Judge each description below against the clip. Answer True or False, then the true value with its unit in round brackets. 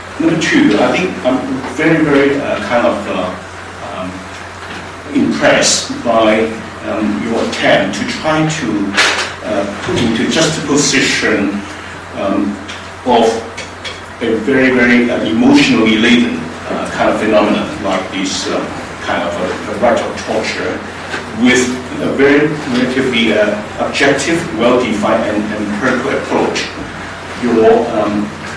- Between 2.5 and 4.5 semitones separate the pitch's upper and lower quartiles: False (5.1 semitones)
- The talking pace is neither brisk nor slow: False (130 wpm)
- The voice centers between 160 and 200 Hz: False (110 Hz)